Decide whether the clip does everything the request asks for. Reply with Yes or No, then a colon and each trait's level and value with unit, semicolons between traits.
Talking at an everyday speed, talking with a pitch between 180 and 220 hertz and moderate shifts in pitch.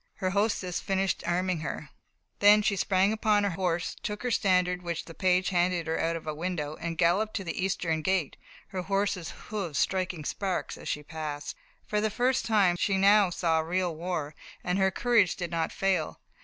Yes: average, 190 wpm; medium, 185 Hz; average, 3.0 semitones